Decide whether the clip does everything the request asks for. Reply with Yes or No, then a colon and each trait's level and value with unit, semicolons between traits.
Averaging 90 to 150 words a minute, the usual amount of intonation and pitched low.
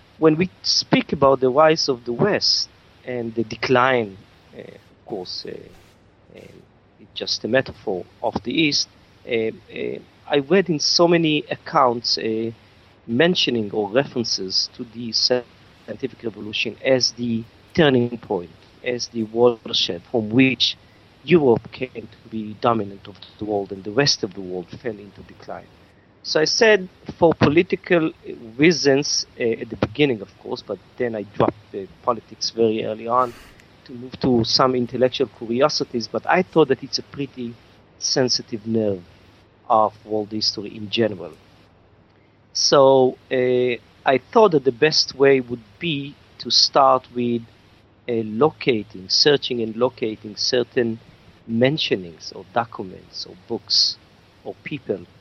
Yes: average, 145 wpm; average, 4.0 semitones; low, 115 Hz